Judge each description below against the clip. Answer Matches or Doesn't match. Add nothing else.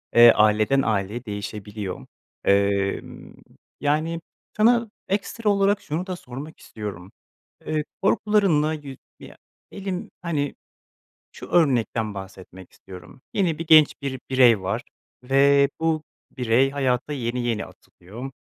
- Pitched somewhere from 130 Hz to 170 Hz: Matches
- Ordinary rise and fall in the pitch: Doesn't match